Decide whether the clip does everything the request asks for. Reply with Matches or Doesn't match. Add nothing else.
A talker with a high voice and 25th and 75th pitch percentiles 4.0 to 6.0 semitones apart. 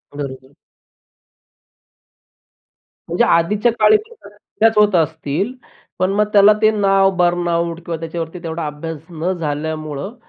Doesn't match